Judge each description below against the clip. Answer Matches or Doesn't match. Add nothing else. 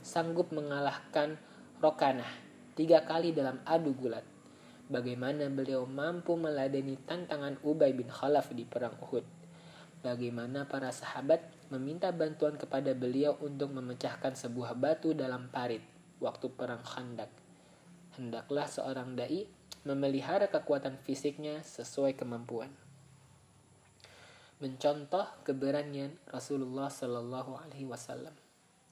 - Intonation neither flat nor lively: Matches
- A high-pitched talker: Doesn't match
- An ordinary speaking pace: Matches